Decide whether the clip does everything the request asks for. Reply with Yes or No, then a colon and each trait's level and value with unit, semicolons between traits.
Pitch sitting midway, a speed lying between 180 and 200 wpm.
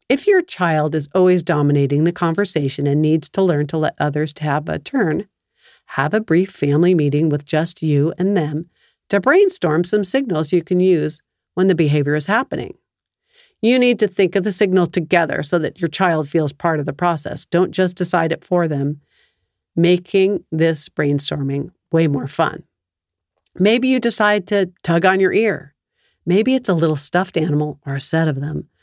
Yes: medium, 170 Hz; average, 185 wpm